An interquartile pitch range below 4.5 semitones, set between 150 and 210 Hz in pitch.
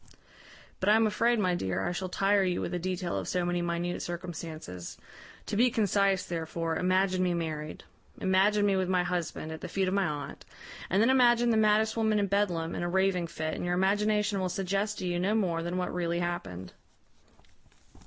Yes: average, 2.9 semitones; medium, 185 Hz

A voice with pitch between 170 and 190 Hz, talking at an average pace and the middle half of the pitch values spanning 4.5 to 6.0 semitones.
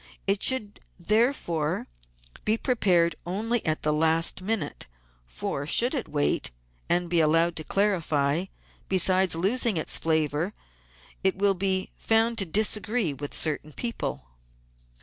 No: medium, 185 Hz; slow, 130 wpm; average, 5.1 semitones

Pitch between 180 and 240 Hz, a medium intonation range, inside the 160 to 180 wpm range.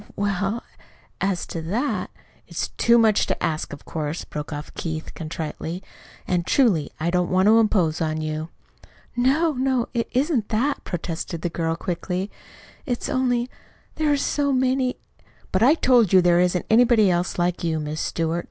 No: high, 190 Hz; wide, 6.8 semitones; average, 170 wpm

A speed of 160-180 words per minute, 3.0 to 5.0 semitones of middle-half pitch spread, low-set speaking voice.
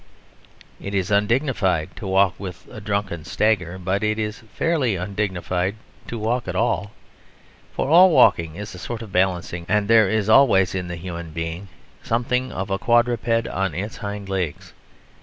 Yes: average, 165 wpm; average, 3.4 semitones; low, 100 Hz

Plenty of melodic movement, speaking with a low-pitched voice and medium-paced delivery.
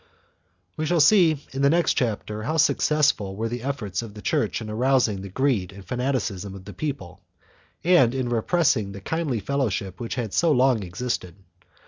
Yes: wide, 5.7 semitones; low, 120 Hz; average, 180 wpm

